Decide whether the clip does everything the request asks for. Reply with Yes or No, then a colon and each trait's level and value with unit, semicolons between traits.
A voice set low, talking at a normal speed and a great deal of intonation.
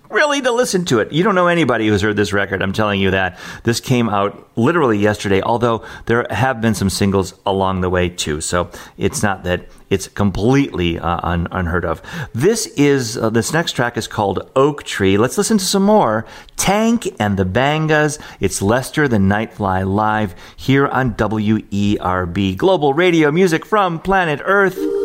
Yes: low, 110 Hz; average, 185 wpm; wide, 7.0 semitones